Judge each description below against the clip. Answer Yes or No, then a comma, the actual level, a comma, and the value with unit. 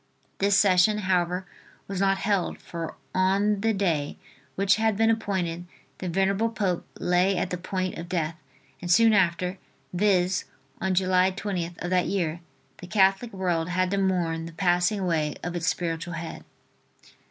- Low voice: No, medium, 185 Hz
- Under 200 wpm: Yes, average, 160 wpm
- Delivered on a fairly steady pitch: Yes, narrow, 2.1 semitones